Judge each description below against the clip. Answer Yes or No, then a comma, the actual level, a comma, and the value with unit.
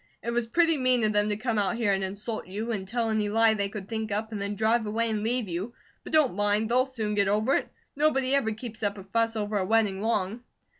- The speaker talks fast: Yes, fast, 255 wpm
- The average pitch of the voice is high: Yes, high, 220 Hz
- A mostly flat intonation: Yes, narrow, 2.3 semitones